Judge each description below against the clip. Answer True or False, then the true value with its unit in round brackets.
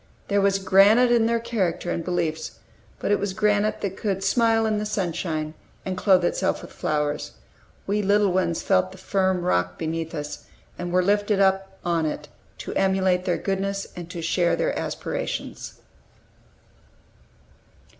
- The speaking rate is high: False (155 wpm)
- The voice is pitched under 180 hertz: False (190 Hz)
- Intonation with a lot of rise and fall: False (2.8 semitones)